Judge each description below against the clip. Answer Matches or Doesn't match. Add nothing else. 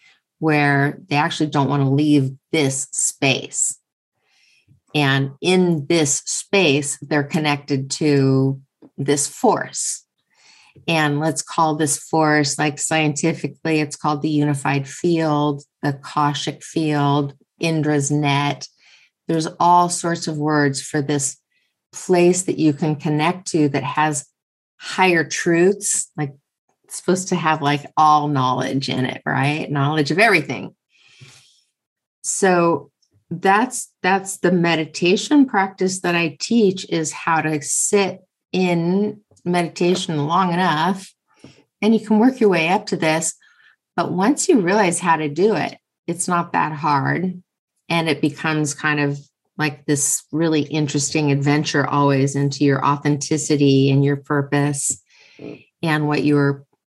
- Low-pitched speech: Doesn't match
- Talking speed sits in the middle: Doesn't match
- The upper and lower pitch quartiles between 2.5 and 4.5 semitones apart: Matches